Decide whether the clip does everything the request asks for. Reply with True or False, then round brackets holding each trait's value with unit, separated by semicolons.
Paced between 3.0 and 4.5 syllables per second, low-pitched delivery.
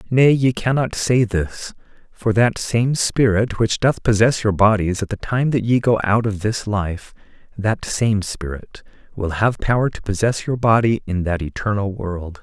True (4.4 syllables/s; 110 Hz)